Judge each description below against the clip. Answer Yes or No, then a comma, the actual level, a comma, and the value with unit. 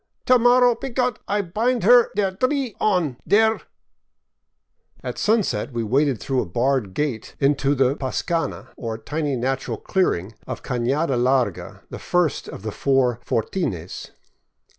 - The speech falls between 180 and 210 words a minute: No, average, 150 wpm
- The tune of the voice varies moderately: No, wide, 9.0 semitones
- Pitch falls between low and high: Yes, medium, 145 Hz